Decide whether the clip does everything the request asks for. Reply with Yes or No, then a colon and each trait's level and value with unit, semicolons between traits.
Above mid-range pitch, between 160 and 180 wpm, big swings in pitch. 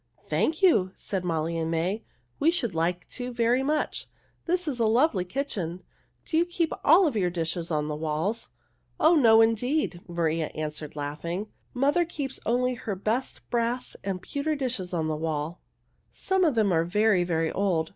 Yes: high, 205 Hz; average, 175 wpm; wide, 8.0 semitones